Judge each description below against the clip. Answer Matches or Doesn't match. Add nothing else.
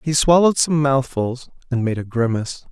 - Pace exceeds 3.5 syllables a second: Matches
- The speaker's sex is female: Doesn't match